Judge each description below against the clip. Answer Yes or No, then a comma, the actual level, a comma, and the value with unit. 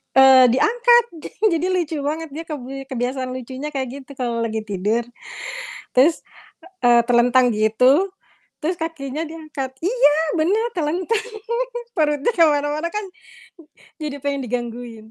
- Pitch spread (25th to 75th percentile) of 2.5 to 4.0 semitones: No, average, 4.7 semitones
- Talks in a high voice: Yes, very high, 280 Hz